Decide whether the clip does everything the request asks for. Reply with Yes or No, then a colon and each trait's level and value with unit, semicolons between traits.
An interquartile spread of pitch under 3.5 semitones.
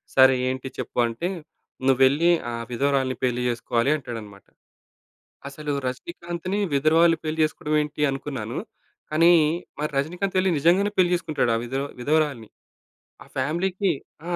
No: average, 4.7 semitones